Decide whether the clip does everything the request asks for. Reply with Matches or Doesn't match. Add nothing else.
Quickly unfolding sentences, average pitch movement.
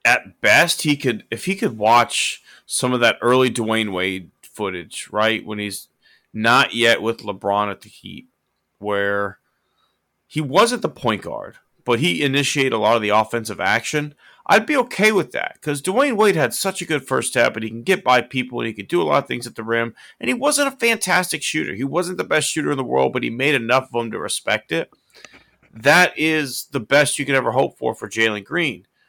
Doesn't match